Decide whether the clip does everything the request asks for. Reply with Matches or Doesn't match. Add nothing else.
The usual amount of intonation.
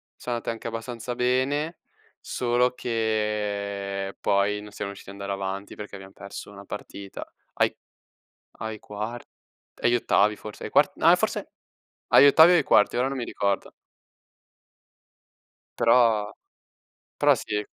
Matches